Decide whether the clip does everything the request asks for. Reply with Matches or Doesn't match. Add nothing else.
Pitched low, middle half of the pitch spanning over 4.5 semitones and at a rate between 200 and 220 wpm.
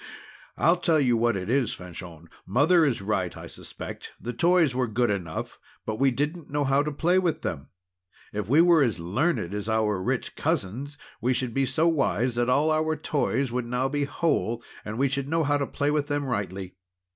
Matches